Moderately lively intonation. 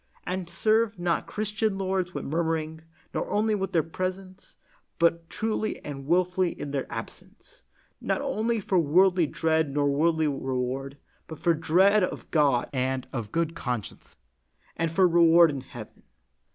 Yes: average, 4.4 semitones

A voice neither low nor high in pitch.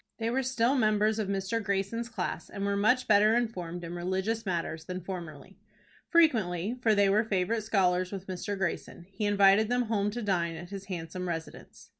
No: high, 200 Hz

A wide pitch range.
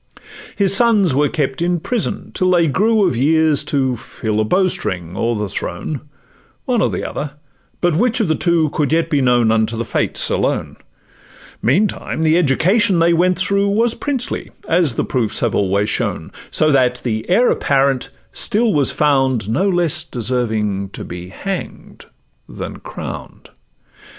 Yes: wide, 7.1 semitones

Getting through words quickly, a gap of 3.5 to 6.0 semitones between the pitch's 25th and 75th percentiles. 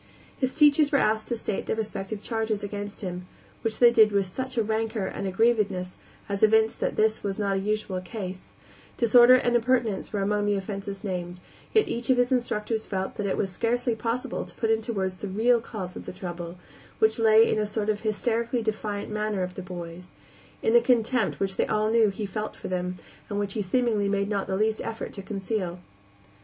No: fast, 210 wpm; average, 2.7 semitones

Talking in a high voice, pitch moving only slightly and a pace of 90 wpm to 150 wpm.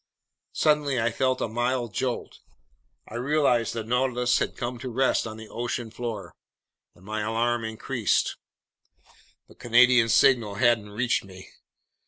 No: low, 120 Hz; narrow, 2.1 semitones; slow, 135 wpm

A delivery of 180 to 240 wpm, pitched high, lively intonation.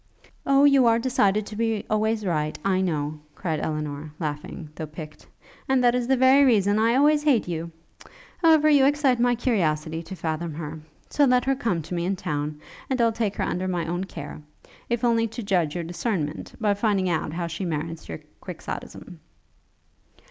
Yes: average, 185 wpm; high, 195 Hz; wide, 6.9 semitones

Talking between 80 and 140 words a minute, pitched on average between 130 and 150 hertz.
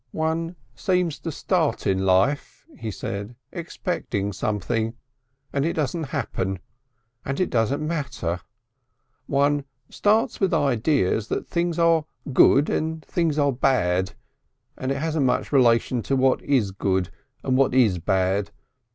Yes: slow, 135 wpm; low, 135 Hz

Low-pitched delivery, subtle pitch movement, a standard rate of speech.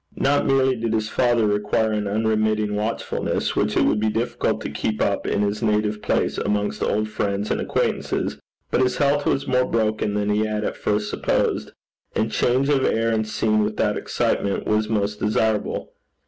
Yes: low, 110 Hz; narrow, 1.5 semitones; average, 180 wpm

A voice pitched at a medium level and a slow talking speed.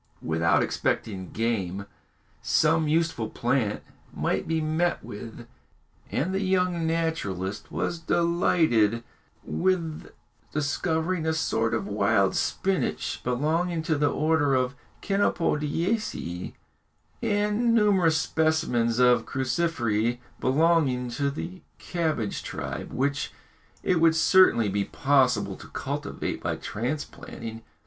Yes: medium, 150 Hz; slow, 105 wpm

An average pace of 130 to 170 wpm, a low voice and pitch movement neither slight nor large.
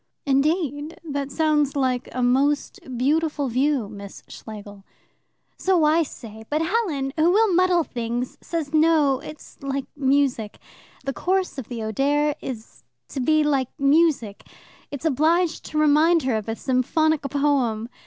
No: average, 145 wpm; very high, 285 Hz; average, 3.7 semitones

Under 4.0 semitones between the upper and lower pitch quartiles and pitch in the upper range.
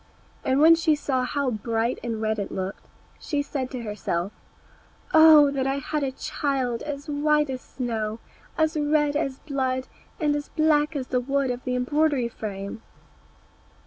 Yes: average, 3.5 semitones; very high, 270 Hz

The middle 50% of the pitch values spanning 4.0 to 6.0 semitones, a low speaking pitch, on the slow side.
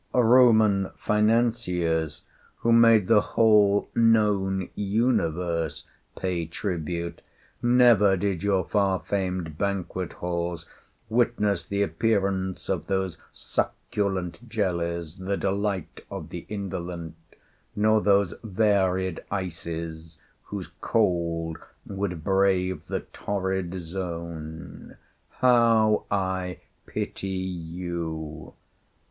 No: average, 3.3 semitones; very low, 95 Hz; slow, 90 wpm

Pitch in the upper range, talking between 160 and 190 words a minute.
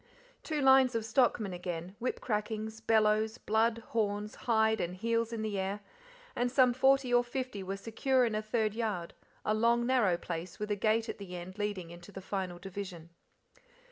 Yes: high, 215 Hz; average, 180 wpm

